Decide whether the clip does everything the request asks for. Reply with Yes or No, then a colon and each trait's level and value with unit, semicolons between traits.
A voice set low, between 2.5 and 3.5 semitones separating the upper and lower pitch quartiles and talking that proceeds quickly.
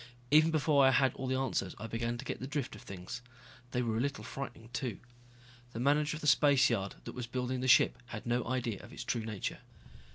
Yes: low, 125 Hz; average, 3.0 semitones; fast, 225 wpm